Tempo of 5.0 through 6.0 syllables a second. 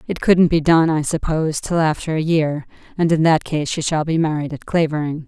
Yes: 5.4 syllables/s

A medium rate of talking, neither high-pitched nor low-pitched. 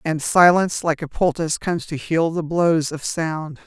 Yes: average, 195 wpm; medium, 160 Hz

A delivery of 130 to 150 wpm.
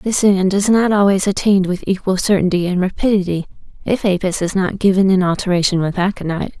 No: average, 180 wpm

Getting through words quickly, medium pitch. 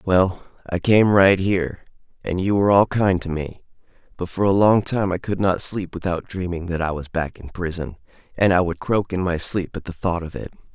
No: fast, 230 wpm; very low, 90 Hz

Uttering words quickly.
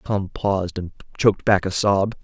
No: average, 190 wpm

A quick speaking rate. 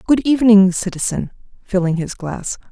No: slow, 135 wpm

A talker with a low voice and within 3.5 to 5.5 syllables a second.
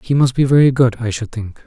No: low, 125 Hz; 5.9 syllables/s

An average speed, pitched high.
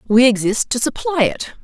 Yes: average, 185 wpm; high, 245 Hz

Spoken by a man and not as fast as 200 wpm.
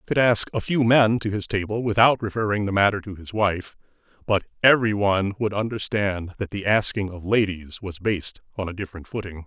No: male; fast, 205 wpm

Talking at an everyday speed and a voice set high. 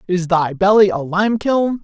Yes: average, 195 wpm; high, 195 Hz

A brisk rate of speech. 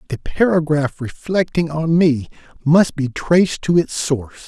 No: average, 145 wpm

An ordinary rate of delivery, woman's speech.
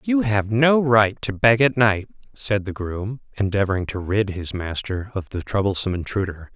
No: average, 185 wpm; male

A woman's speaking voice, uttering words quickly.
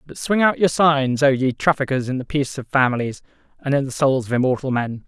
No: male; fast, 235 wpm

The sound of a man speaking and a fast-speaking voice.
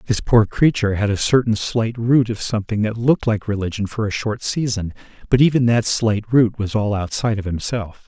Yes: male; fast, 210 wpm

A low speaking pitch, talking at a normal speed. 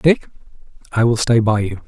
Yes: low, 115 Hz; average, 190 wpm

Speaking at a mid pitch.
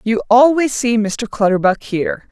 No: high, 230 Hz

